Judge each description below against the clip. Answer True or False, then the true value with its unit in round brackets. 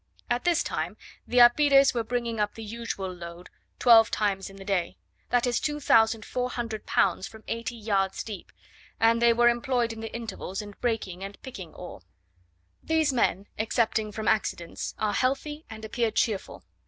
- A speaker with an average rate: True (165 wpm)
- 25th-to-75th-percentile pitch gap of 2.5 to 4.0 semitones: True (2.9 semitones)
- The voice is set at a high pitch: True (225 Hz)